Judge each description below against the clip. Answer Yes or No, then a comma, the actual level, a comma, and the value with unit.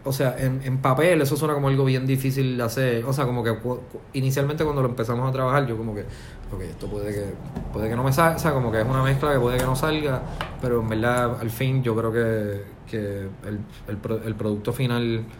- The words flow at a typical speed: No, fast, 240 wpm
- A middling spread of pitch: Yes, average, 3.2 semitones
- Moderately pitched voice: No, low, 125 Hz